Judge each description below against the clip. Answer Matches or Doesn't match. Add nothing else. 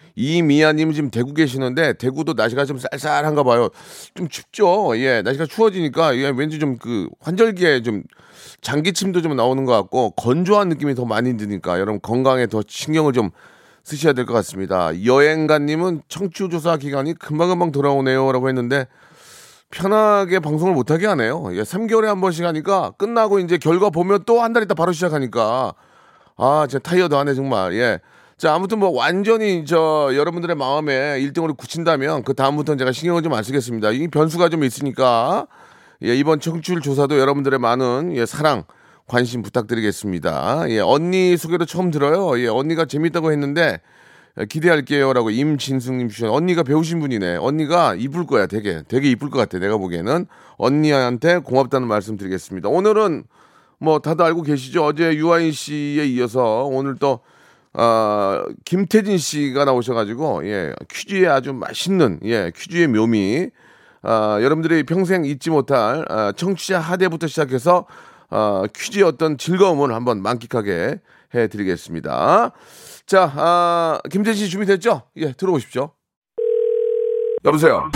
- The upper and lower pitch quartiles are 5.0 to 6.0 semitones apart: Matches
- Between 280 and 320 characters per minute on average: Doesn't match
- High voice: Doesn't match